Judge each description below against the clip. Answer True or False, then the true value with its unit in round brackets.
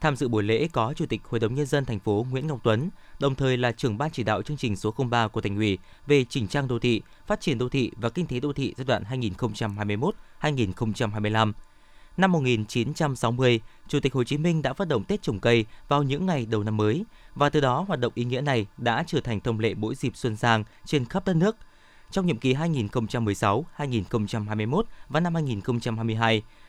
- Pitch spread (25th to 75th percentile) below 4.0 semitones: False (4.7 semitones)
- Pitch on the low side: True (125 Hz)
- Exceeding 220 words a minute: False (210 wpm)